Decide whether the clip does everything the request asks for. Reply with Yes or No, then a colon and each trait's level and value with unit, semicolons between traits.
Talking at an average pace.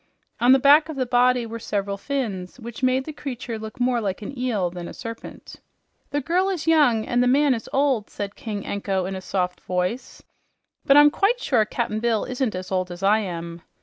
No: fast, 215 wpm